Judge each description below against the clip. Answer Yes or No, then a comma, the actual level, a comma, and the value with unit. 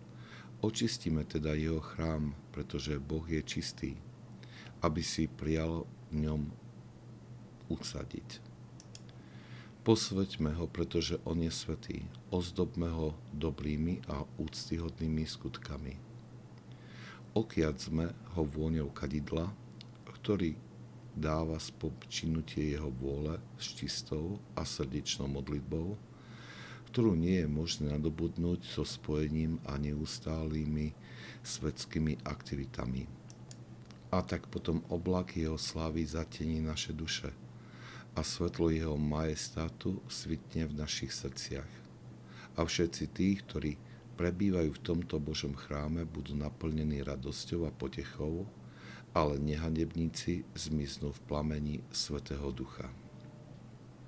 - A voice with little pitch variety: Yes, narrow, 2.1 semitones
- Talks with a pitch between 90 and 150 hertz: No, very low, 80 Hz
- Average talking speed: No, slow, 100 wpm